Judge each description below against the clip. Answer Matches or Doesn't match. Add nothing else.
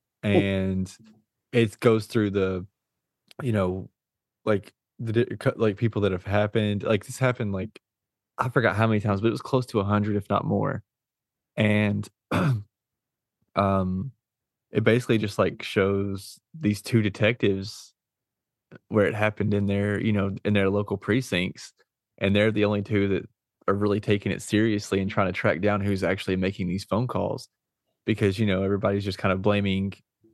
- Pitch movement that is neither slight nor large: Doesn't match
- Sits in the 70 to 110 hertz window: Matches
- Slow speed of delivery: Doesn't match